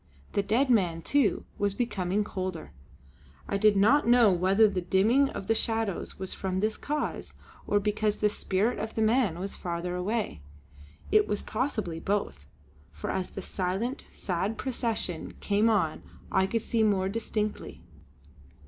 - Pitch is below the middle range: No, high, 205 Hz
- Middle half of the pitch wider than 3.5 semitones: No, average, 3.1 semitones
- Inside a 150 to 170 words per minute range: Yes, average, 155 wpm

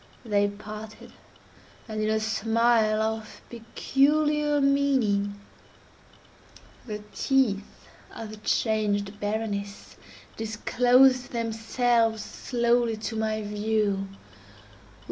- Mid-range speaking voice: No, high, 220 Hz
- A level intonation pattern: Yes, narrow, 2.3 semitones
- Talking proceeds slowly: Yes, slow, 85 wpm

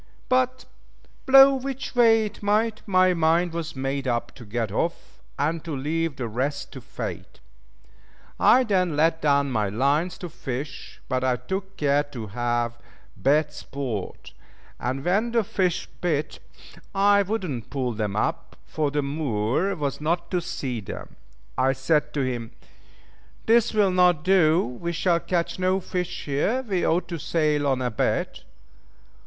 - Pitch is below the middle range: No, medium, 155 Hz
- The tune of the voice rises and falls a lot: Yes, wide, 5.8 semitones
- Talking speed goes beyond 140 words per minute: Yes, average, 160 wpm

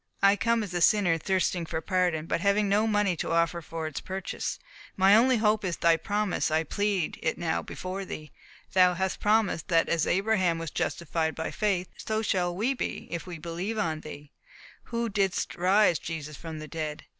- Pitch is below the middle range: No, medium, 180 Hz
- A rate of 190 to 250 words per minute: Yes, average, 195 wpm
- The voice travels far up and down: No, average, 3.8 semitones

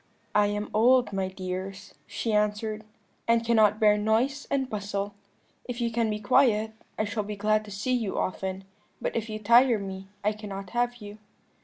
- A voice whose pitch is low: No, high, 210 Hz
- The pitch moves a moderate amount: No, narrow, 2.3 semitones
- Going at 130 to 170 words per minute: No, average, 180 wpm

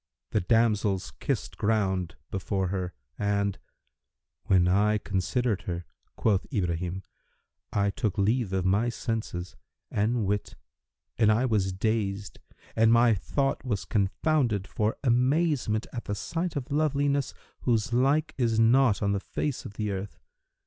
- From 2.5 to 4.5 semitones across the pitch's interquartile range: Yes, average, 3.8 semitones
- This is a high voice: No, low, 105 Hz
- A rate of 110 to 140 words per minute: Yes, slow, 135 wpm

